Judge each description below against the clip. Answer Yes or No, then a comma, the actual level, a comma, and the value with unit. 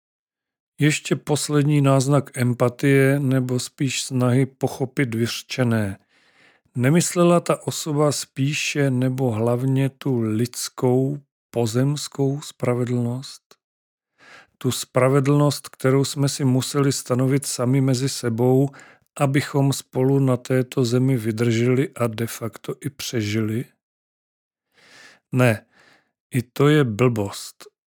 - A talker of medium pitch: No, low, 130 Hz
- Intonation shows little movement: Yes, narrow, 2.3 semitones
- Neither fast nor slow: No, slow, 95 wpm